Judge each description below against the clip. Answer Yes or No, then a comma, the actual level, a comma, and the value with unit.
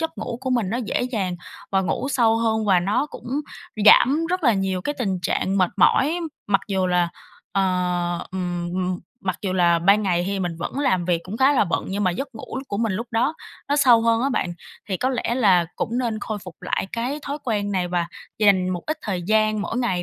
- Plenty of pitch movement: No, average, 4.6 semitones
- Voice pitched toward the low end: No, high, 205 Hz